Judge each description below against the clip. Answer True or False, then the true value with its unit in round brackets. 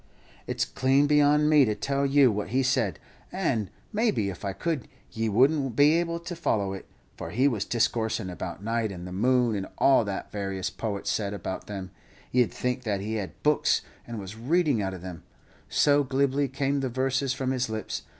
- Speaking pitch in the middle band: False (120 Hz)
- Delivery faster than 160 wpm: True (200 wpm)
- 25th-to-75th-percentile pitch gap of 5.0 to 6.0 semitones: True (5.4 semitones)